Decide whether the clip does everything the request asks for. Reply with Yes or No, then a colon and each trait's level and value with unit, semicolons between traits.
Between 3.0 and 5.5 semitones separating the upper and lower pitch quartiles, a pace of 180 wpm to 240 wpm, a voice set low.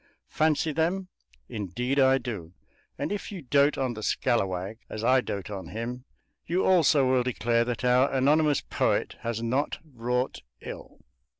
No: average, 3.9 semitones; average, 155 wpm; low, 125 Hz